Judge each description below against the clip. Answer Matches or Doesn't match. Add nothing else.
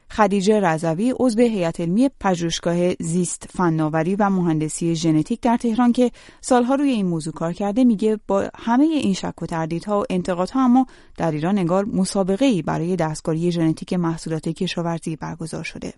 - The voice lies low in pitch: Doesn't match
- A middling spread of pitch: Doesn't match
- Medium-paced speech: Doesn't match